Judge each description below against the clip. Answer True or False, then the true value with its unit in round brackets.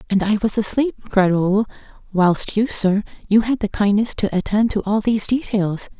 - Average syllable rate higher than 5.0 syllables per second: False (4.9 syllables/s)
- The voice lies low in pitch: False (205 Hz)